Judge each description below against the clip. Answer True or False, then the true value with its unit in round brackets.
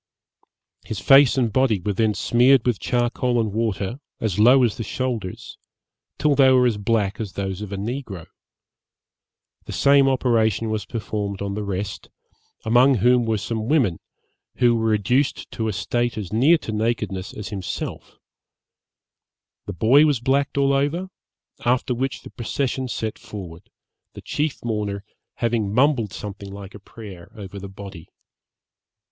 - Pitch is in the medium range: False (110 Hz)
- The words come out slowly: False (155 wpm)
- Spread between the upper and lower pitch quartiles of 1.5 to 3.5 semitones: False (4.0 semitones)